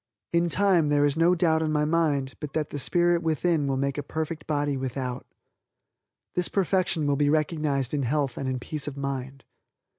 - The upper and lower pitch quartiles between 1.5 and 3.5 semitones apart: Yes, average, 3.0 semitones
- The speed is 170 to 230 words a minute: Yes, average, 190 wpm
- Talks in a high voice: No, medium, 150 Hz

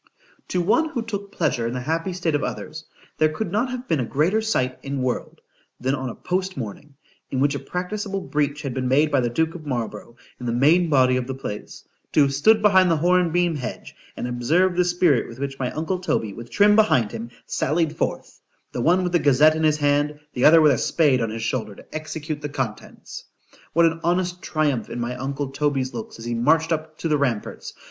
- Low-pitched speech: No, medium, 150 Hz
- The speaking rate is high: Yes, fast, 215 wpm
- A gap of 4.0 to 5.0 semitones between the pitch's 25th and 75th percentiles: No, wide, 5.4 semitones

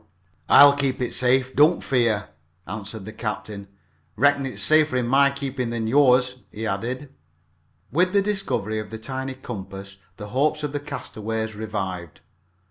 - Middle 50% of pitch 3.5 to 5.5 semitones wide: Yes, average, 4.4 semitones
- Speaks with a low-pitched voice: Yes, low, 125 Hz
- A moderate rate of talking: Yes, average, 155 wpm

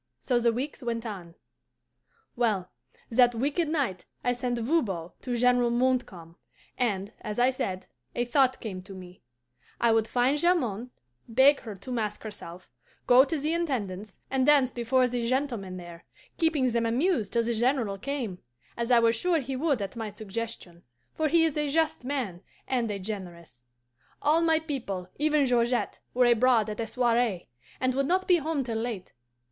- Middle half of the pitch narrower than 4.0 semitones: No, average, 4.3 semitones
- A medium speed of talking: Yes, average, 175 wpm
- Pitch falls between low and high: No, high, 240 Hz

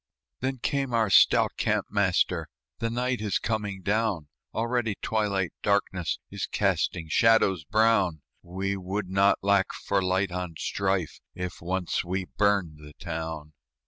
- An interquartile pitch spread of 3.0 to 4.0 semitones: Yes, average, 3.4 semitones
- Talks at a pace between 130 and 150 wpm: Yes, average, 140 wpm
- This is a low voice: Yes, very low, 95 Hz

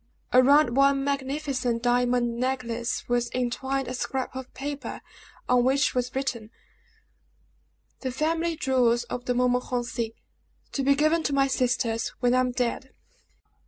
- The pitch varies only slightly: Yes, narrow, 2.0 semitones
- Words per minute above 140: No, slow, 135 wpm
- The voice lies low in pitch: No, very high, 255 Hz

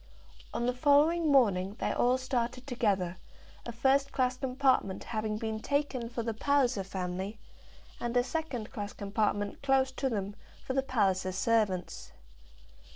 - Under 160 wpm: Yes, average, 145 wpm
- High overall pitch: Yes, high, 235 Hz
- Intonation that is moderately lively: Yes, average, 4.5 semitones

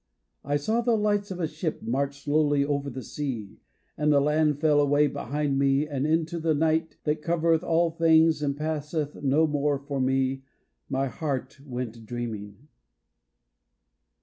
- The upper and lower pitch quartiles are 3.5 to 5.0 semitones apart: No, narrow, 2.6 semitones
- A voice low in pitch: No, medium, 145 Hz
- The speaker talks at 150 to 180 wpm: Yes, average, 155 wpm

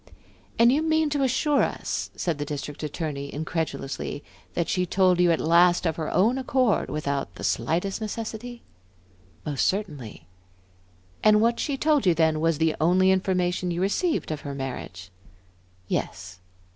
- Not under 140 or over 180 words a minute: Yes, average, 155 wpm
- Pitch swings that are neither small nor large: No, wide, 6.3 semitones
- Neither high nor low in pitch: Yes, medium, 175 Hz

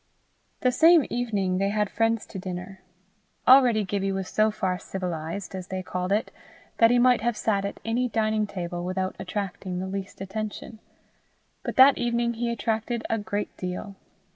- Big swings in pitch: No, average, 3.4 semitones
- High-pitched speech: Yes, high, 205 Hz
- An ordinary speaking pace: Yes, average, 165 wpm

